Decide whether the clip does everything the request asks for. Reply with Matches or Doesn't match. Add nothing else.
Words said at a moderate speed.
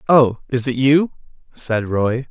Matches